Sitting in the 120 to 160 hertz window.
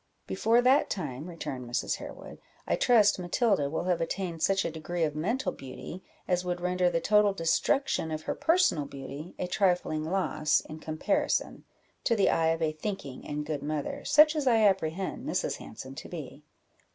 No: medium, 175 Hz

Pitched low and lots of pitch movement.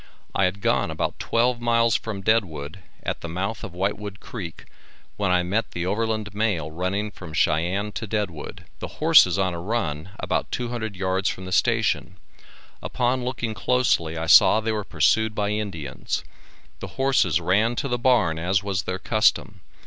No: low, 100 Hz; average, 3.8 semitones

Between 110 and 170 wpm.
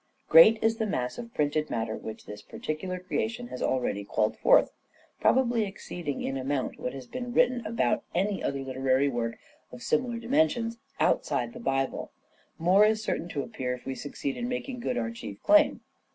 No: average, 195 wpm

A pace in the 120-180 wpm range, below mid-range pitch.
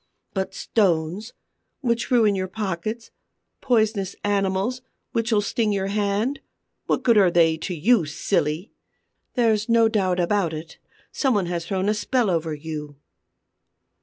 No: slow, 135 wpm; high, 200 Hz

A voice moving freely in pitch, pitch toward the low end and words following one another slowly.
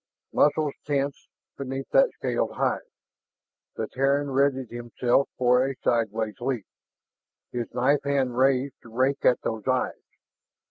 No: narrow, 2.5 semitones; low, 130 Hz; slow, 130 wpm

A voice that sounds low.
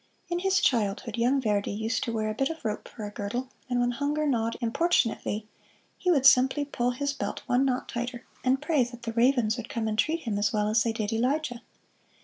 No: high, 245 Hz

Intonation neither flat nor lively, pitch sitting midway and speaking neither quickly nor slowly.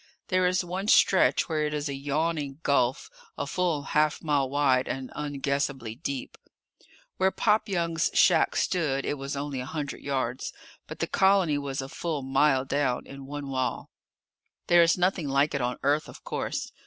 Yes: average, 3.3 semitones; medium, 145 Hz; average, 175 wpm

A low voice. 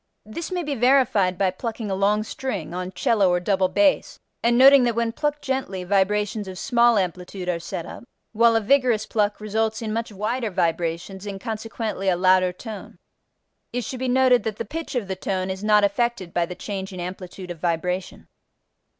No: high, 210 Hz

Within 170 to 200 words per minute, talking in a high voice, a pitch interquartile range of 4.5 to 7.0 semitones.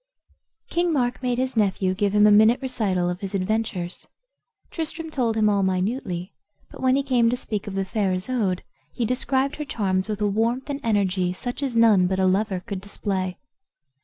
Yes: average, 190 wpm; high, 210 Hz; average, 4.8 semitones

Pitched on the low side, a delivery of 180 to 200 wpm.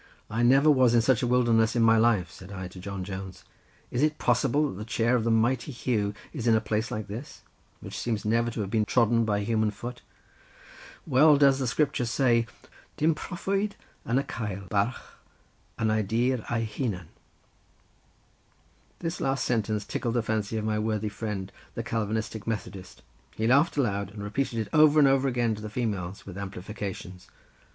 Yes: low, 115 Hz; average, 185 wpm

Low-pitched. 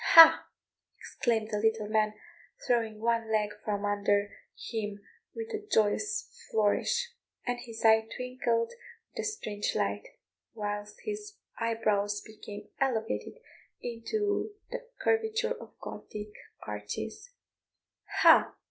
No: high, 225 Hz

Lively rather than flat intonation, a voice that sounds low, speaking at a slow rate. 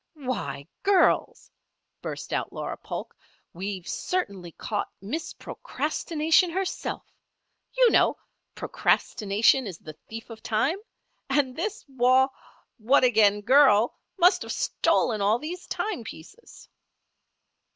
No: wide, 7.9 semitones; very high, 250 Hz; slow, 110 wpm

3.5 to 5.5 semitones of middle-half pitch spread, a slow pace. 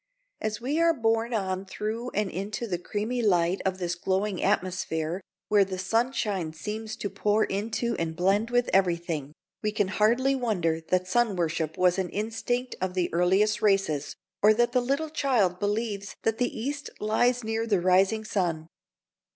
No: average, 3.8 semitones; average, 165 wpm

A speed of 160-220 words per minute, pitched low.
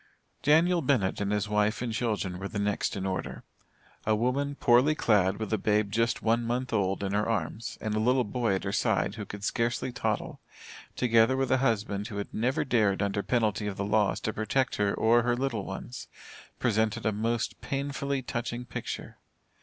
Yes: average, 195 wpm; low, 110 Hz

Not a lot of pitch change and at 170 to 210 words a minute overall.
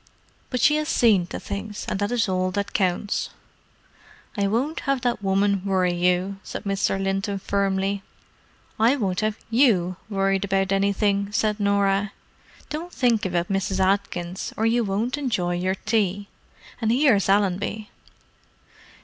No: narrow, 2.3 semitones; average, 145 wpm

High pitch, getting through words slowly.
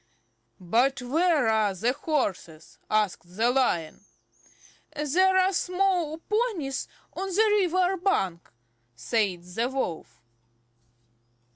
Yes: very high, 265 Hz; slow, 100 wpm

